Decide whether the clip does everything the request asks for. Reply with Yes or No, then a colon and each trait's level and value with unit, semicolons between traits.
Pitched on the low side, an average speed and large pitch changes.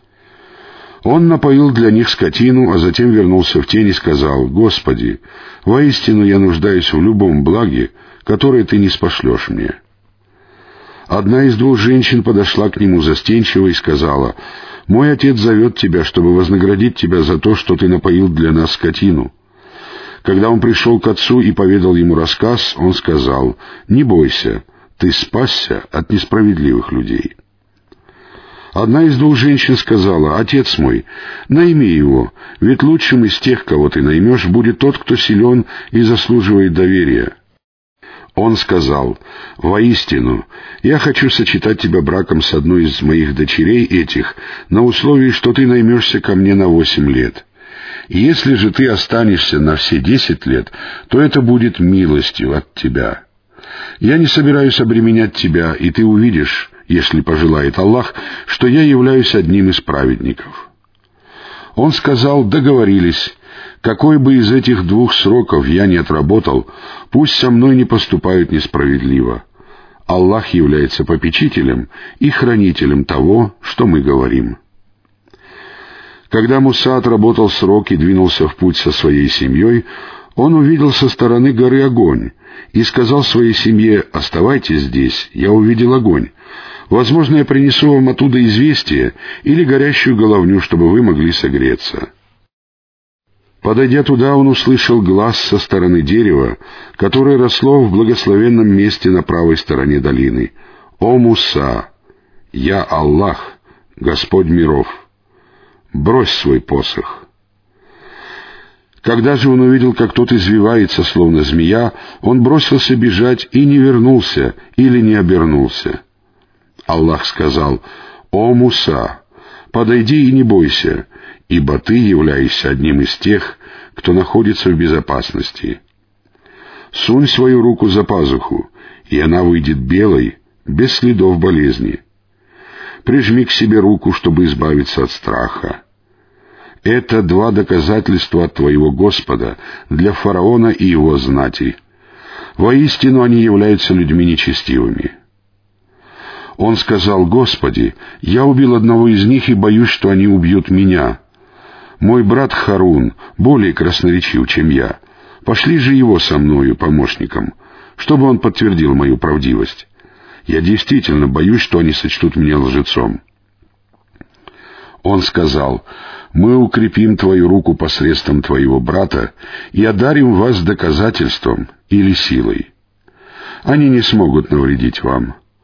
Yes: low, 105 Hz; average, 125 wpm; wide, 5.9 semitones